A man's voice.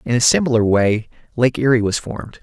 Yes: male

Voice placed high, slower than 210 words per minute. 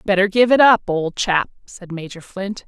Yes: high, 195 Hz; average, 200 wpm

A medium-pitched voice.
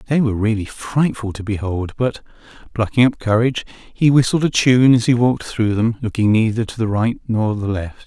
No: low, 115 Hz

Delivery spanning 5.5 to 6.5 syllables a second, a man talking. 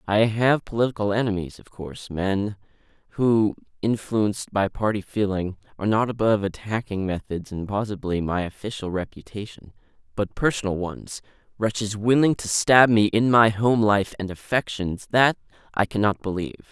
No: 5.1 syllables/s; male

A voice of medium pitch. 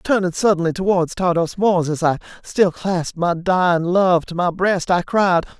Yes: medium, 180 Hz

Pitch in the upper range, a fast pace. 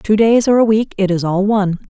Yes: high, 205 Hz; fast, 285 wpm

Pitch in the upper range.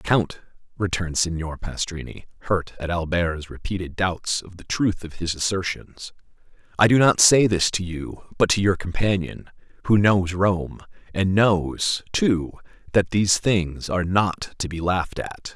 No: very low, 90 Hz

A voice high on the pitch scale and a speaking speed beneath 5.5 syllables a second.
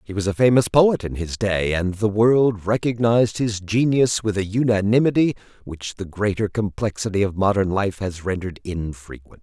No: low, 105 Hz; 5.0 syllables/s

